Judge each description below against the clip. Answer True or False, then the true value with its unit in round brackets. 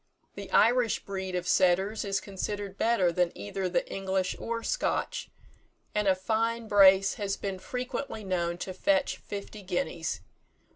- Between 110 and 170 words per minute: True (145 wpm)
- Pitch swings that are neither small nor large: True (3.1 semitones)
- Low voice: False (195 Hz)